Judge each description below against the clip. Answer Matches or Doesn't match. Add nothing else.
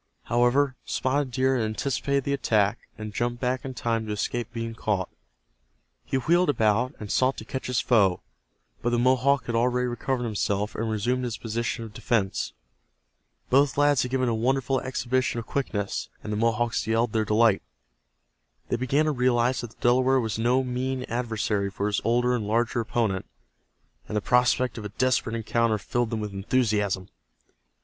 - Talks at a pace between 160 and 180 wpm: Matches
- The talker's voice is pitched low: Matches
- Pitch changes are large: Doesn't match